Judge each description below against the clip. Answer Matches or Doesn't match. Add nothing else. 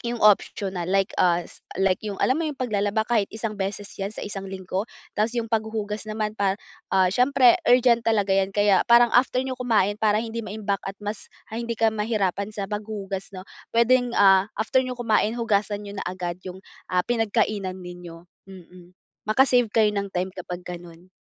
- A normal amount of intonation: Matches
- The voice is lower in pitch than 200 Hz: Doesn't match